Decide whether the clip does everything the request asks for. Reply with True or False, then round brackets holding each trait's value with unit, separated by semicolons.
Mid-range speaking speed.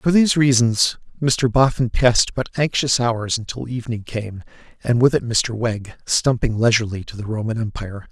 True (170 wpm)